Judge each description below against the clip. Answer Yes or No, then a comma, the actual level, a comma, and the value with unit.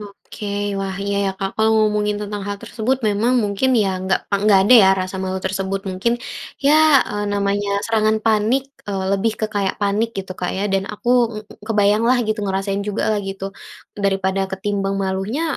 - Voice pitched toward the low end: No, high, 200 Hz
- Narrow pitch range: Yes, narrow, 1.8 semitones